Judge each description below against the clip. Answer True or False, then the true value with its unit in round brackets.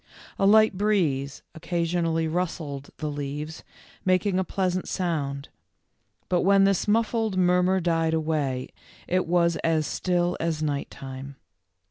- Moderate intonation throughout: True (3.5 semitones)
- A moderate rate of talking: False (130 wpm)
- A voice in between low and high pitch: True (170 Hz)